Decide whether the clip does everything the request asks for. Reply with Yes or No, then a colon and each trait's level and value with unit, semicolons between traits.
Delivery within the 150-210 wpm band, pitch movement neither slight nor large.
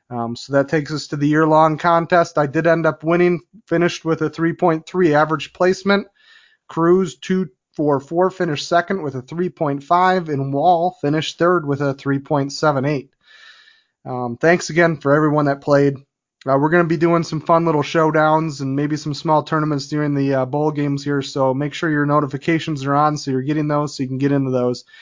Yes: average, 195 wpm; average, 3.2 semitones